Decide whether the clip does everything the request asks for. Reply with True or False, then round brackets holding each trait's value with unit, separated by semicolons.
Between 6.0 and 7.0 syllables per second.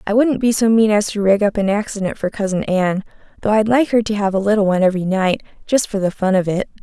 True (6.4 syllables/s)